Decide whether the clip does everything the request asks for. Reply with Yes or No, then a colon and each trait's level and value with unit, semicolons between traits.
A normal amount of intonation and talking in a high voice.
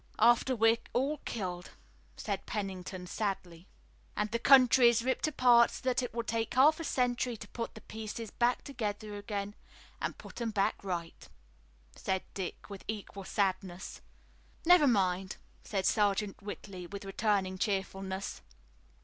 Yes: average, 3.6 semitones; high, 210 Hz